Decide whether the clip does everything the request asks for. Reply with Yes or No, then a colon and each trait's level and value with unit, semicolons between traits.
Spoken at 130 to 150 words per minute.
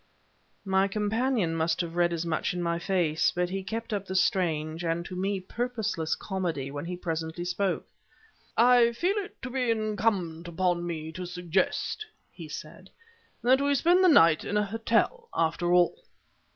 No: average, 170 wpm